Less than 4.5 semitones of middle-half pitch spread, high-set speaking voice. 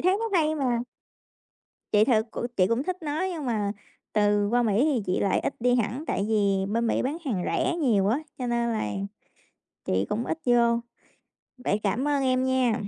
Yes: average, 4.1 semitones; high, 235 Hz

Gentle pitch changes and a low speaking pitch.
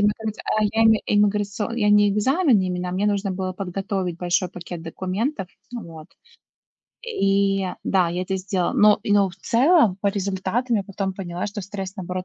No: narrow, 2.2 semitones; high, 195 Hz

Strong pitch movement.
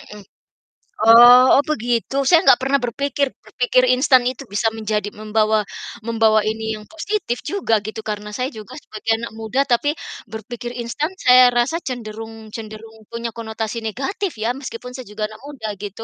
No: average, 2.7 semitones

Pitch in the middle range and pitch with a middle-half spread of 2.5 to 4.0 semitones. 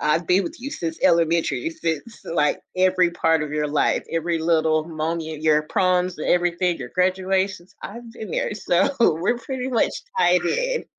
Yes: medium, 175 Hz; average, 3.0 semitones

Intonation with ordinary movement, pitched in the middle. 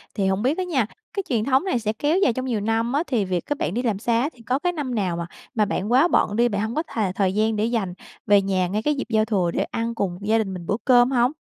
No: average, 4.1 semitones; high, 225 Hz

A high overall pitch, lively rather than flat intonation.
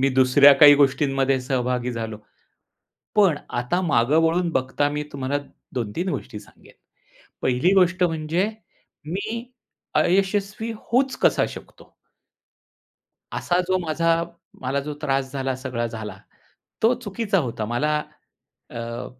No: medium, 145 Hz; wide, 6.0 semitones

